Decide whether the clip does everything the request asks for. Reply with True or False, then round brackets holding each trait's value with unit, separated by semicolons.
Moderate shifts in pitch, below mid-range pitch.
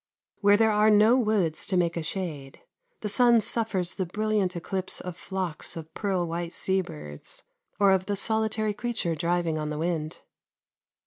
False (4.0 semitones; 190 Hz)